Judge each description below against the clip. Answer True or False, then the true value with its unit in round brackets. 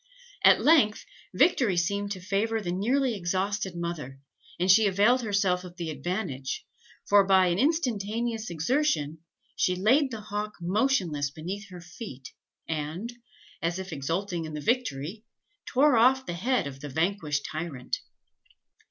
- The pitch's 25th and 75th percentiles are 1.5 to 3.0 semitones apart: False (4.9 semitones)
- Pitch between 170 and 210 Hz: True (190 Hz)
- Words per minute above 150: False (145 wpm)